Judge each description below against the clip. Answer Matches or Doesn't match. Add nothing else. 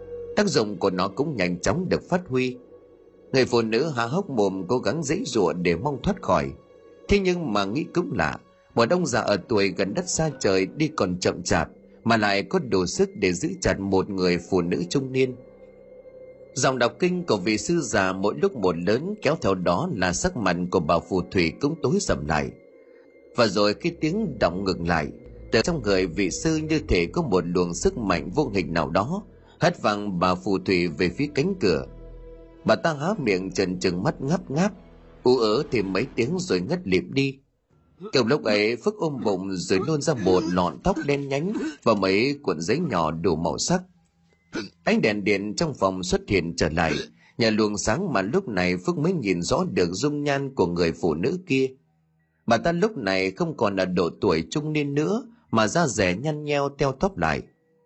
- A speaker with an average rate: Matches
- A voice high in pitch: Doesn't match